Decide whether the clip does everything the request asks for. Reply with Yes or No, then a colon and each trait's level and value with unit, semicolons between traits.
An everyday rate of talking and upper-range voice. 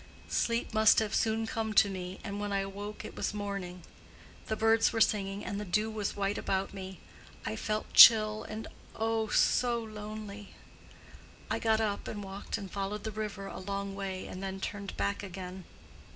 Yes: average, 180 wpm; high, 205 Hz